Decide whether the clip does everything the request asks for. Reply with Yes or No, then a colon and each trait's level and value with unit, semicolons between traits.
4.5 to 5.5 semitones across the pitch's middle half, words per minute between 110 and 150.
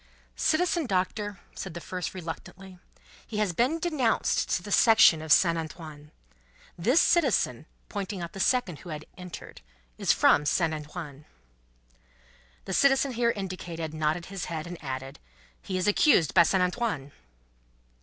Yes: average, 5.1 semitones; average, 145 wpm